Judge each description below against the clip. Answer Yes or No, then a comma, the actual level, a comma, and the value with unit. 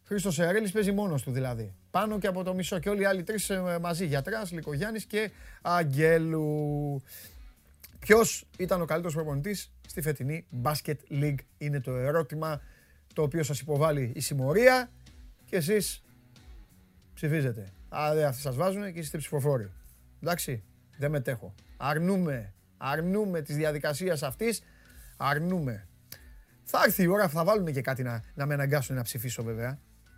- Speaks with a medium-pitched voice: Yes, medium, 150 Hz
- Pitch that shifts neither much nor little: No, wide, 6.0 semitones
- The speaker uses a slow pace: No, average, 145 wpm